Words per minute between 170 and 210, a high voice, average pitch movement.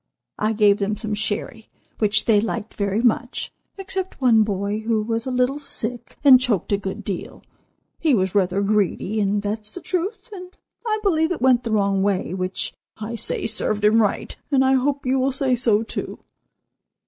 Yes: average, 185 wpm; high, 220 Hz; average, 4.1 semitones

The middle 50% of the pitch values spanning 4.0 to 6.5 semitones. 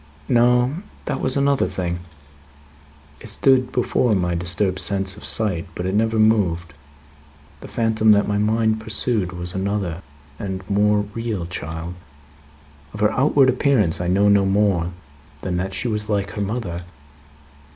No: average, 3.5 semitones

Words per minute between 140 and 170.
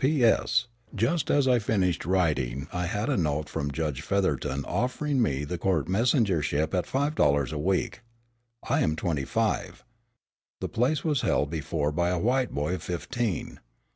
Yes: average, 165 wpm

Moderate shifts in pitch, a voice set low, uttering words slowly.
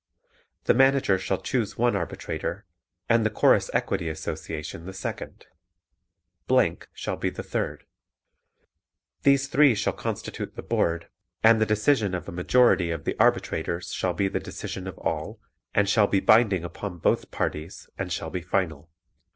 No: average, 4.4 semitones; very low, 95 Hz; average, 150 wpm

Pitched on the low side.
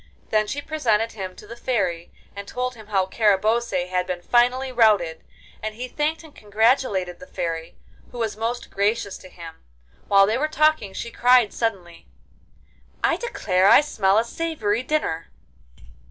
No: high, 215 Hz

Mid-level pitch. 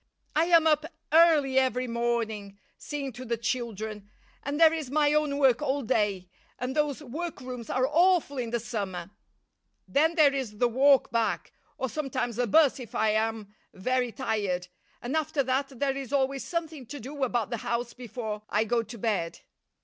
No: very high, 255 Hz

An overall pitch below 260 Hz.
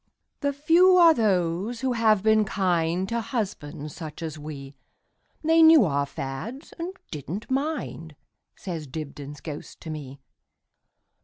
Yes: medium, 185 Hz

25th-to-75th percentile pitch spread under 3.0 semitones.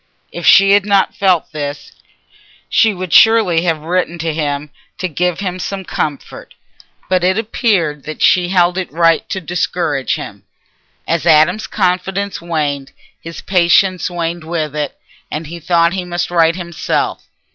Yes: narrow, 2.6 semitones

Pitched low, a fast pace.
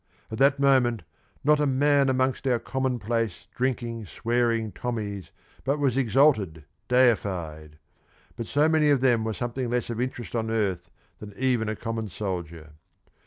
No: low, 120 Hz; average, 155 wpm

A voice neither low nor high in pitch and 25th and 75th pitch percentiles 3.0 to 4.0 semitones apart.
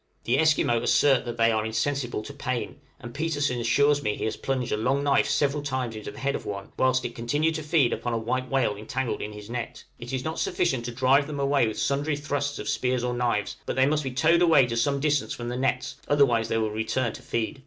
No: low, 130 Hz; average, 3.4 semitones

